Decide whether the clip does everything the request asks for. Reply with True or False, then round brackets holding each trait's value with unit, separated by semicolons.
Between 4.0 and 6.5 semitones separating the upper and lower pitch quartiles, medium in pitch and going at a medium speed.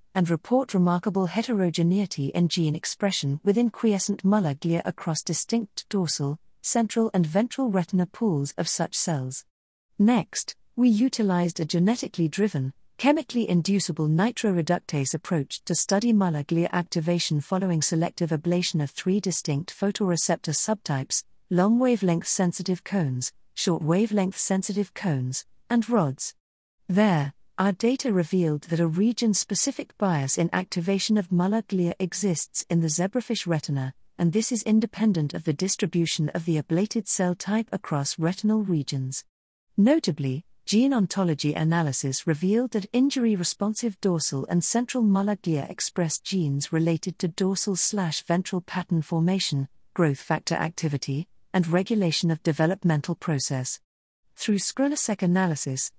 False (4.3 semitones; 180 Hz; 130 wpm)